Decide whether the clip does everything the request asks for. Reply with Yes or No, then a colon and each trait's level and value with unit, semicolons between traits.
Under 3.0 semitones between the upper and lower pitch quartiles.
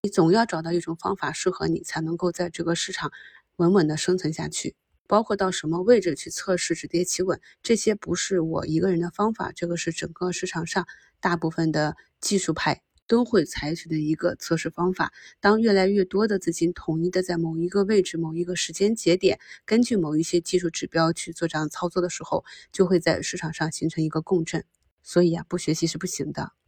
Yes: narrow, 2.4 semitones